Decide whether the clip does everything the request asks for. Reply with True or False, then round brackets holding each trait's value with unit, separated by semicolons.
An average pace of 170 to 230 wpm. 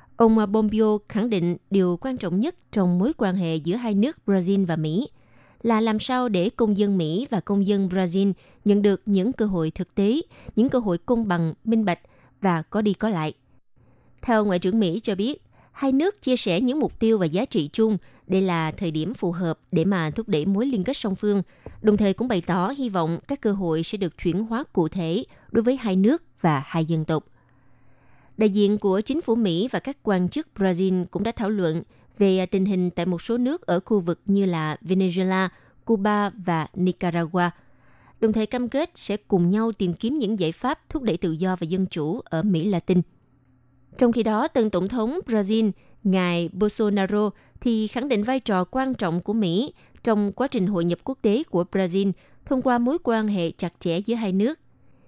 True (210 wpm)